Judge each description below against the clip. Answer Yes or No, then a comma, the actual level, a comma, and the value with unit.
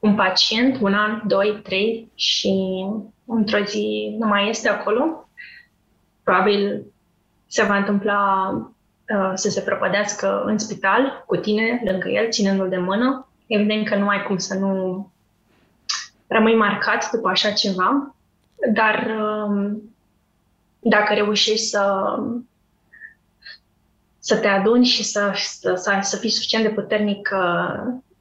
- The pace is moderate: Yes, average, 125 wpm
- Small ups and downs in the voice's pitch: Yes, narrow, 2.0 semitones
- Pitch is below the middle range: No, high, 210 Hz